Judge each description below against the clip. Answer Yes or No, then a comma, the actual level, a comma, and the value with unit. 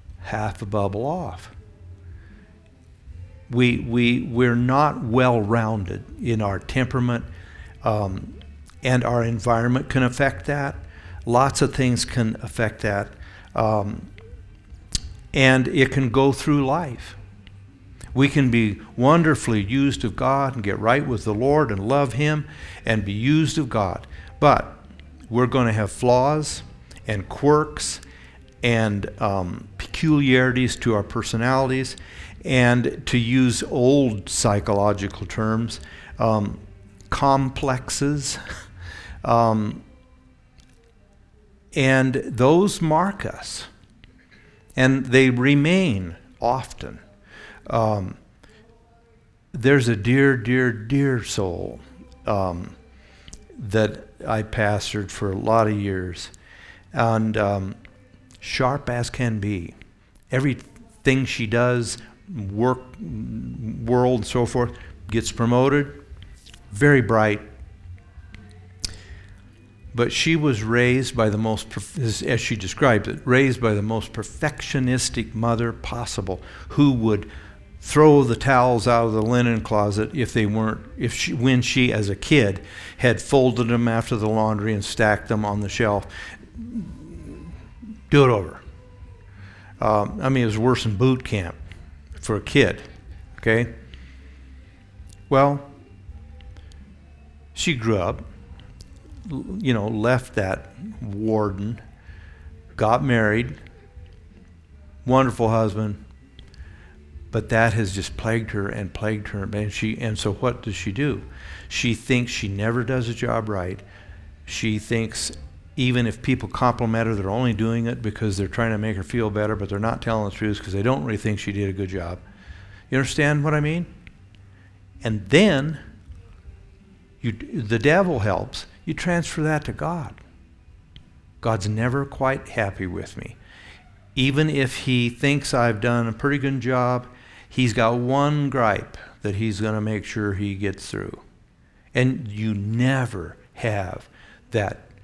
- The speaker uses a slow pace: Yes, slow, 125 wpm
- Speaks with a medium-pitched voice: No, low, 110 Hz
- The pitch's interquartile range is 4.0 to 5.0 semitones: Yes, average, 4.4 semitones